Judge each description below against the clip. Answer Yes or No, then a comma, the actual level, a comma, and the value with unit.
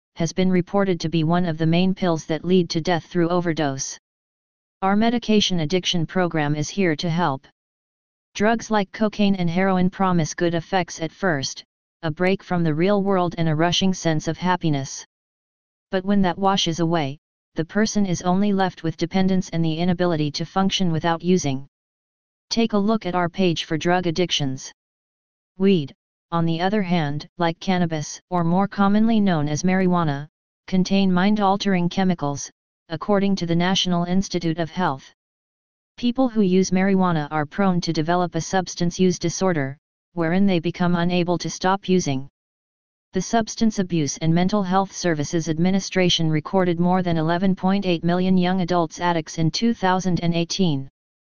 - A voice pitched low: No, medium, 180 Hz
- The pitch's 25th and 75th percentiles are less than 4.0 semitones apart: Yes, narrow, 2.4 semitones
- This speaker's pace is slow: No, average, 160 wpm